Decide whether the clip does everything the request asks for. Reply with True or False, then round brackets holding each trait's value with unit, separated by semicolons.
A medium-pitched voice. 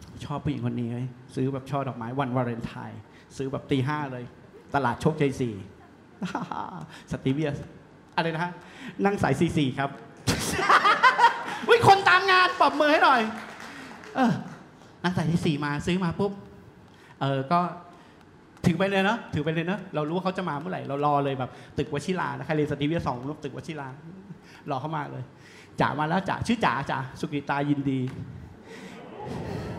True (150 Hz)